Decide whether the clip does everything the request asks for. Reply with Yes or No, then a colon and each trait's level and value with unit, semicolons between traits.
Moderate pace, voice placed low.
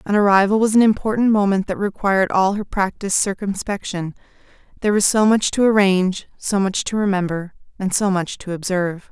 No: average, 180 wpm; high, 195 Hz